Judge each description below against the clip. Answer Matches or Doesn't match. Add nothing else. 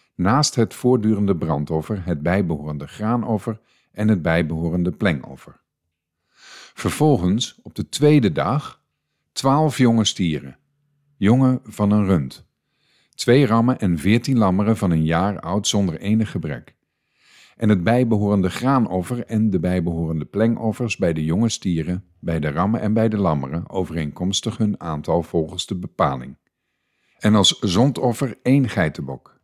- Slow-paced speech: Matches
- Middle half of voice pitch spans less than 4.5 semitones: Doesn't match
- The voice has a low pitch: Matches